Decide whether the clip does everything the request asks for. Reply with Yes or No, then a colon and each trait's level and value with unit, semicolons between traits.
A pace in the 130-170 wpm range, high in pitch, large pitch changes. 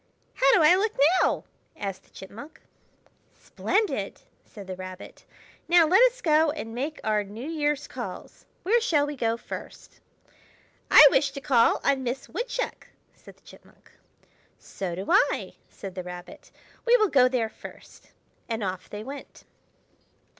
Yes: average, 155 wpm; very high, 270 Hz; wide, 7.4 semitones